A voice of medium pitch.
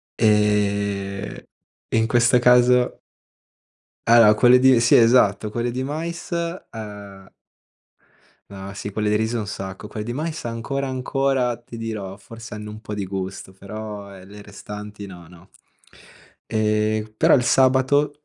No: low, 110 Hz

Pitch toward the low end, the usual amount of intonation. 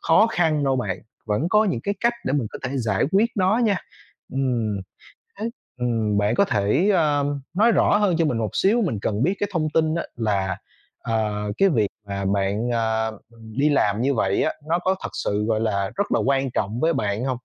No: low, 125 Hz; wide, 8.1 semitones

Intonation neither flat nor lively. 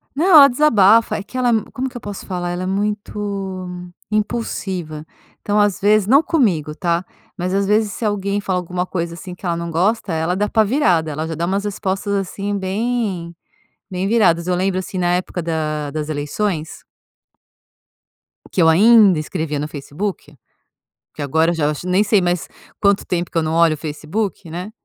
Yes: average, 3.6 semitones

